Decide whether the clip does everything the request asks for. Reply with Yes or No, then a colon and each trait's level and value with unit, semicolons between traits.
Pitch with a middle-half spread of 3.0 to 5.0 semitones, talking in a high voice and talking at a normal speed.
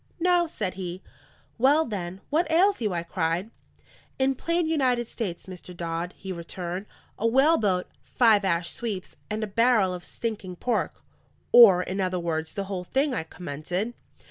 No: wide, 5.5 semitones; high, 200 Hz; average, 160 wpm